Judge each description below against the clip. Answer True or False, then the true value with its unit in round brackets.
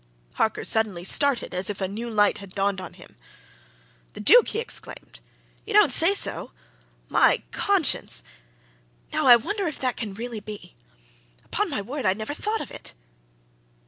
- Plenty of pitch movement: True (6.6 semitones)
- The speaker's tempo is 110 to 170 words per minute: True (165 wpm)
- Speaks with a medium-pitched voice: False (220 Hz)